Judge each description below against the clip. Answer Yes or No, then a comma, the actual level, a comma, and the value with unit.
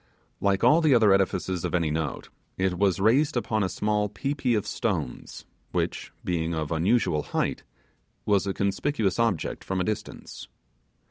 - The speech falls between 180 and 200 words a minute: No, average, 160 wpm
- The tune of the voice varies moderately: Yes, average, 4.2 semitones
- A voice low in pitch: Yes, low, 100 Hz